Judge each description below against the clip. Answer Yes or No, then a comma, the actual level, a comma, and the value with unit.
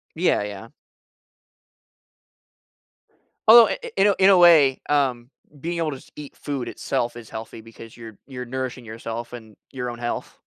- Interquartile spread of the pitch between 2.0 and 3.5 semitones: No, average, 4.6 semitones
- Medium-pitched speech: No, low, 125 Hz